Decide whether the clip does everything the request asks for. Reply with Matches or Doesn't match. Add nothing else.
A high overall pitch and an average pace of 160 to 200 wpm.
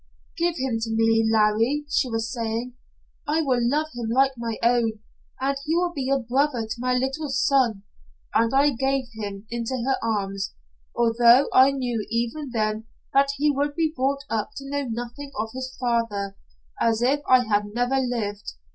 Matches